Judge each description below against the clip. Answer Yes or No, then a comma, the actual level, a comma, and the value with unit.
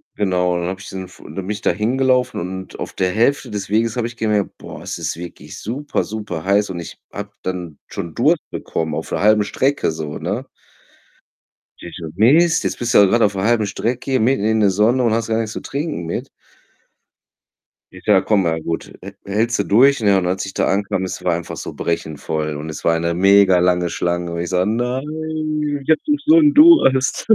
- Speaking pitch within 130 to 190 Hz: No, low, 100 Hz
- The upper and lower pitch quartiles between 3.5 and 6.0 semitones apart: Yes, average, 4.9 semitones